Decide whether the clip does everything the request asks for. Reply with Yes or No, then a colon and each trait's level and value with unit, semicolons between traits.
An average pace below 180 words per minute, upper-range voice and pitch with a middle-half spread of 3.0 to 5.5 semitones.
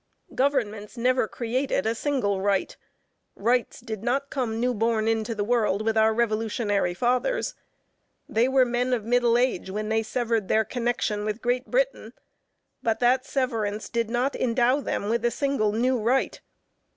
No: average, 160 wpm; high, 235 Hz; narrow, 2.6 semitones